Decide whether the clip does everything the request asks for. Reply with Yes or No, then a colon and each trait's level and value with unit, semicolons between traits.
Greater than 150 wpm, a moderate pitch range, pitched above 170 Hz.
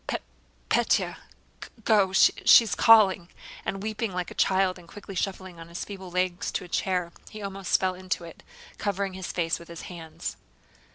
No: average, 180 wpm; narrow, 2.0 semitones; medium, 185 Hz